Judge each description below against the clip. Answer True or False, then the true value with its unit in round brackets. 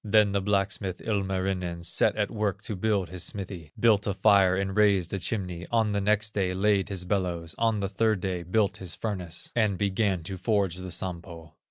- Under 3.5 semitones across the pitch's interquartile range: True (2.4 semitones)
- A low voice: True (95 Hz)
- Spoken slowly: False (195 wpm)